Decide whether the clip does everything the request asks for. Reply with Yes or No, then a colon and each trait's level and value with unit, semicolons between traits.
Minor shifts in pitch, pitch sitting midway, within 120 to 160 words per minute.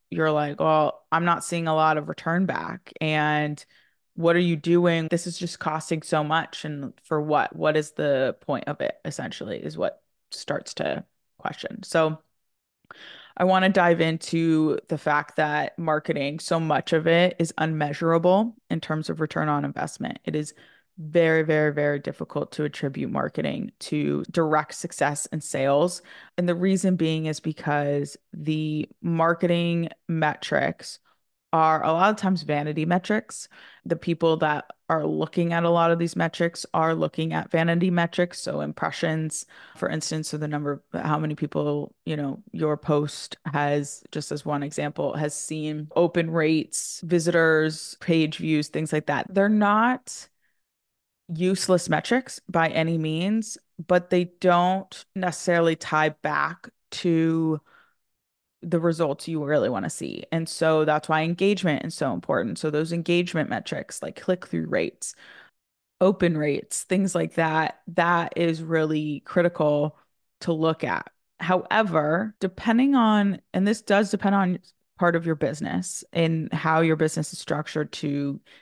Yes: narrow, 2.3 semitones; medium, 160 Hz; average, 155 wpm